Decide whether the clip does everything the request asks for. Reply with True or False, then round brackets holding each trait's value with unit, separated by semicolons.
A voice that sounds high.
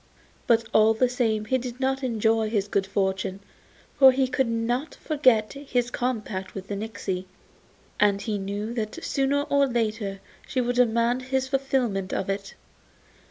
True (230 Hz)